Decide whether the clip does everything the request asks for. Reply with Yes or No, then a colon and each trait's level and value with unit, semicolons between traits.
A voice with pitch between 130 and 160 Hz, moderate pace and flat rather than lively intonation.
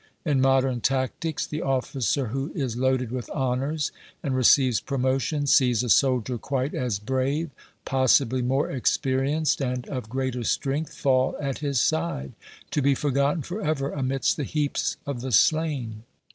Yes: low, 135 Hz; average, 150 wpm; narrow, 2.1 semitones